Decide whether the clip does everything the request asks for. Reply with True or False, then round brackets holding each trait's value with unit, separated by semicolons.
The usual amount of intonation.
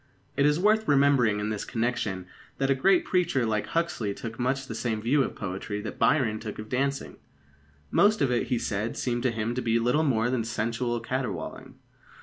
True (3.8 semitones)